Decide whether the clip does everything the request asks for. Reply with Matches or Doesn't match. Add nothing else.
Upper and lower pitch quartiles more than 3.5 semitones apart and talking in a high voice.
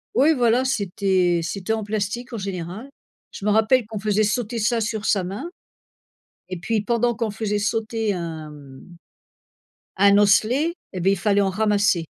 Doesn't match